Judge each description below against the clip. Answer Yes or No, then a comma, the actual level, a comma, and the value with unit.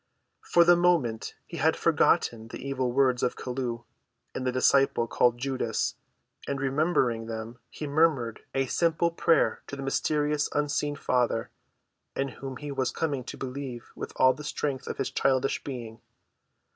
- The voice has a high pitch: No, low, 135 Hz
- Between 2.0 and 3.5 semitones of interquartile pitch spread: Yes, average, 3.1 semitones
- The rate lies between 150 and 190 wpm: Yes, average, 160 wpm